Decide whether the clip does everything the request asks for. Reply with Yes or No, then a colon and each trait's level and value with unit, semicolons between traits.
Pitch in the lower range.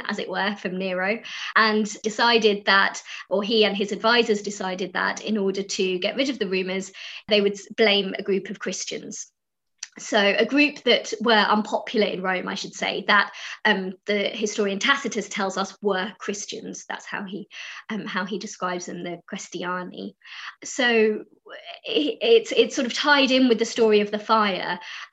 No: high, 210 Hz